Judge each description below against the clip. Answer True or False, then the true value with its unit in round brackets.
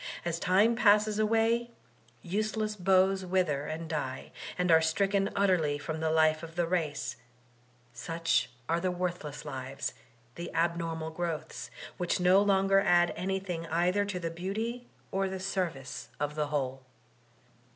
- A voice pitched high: False (175 Hz)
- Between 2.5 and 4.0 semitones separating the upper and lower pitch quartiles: True (3.4 semitones)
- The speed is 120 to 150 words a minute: True (140 wpm)